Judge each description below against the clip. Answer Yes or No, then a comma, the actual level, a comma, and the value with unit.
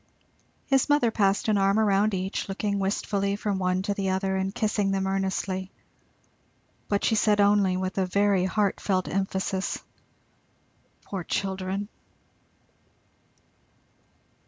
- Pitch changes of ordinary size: No, narrow, 1.2 semitones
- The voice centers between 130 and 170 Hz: No, high, 195 Hz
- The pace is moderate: No, slow, 125 wpm